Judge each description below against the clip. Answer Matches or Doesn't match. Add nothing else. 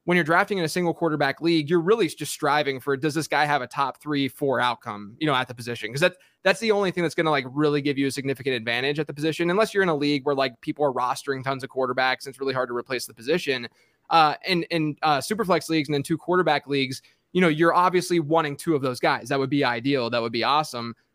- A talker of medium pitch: Matches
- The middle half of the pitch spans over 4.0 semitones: Doesn't match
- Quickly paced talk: Matches